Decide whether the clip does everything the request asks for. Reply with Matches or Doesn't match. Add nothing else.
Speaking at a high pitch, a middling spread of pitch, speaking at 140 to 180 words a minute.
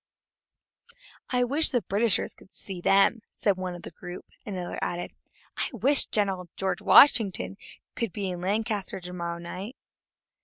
Matches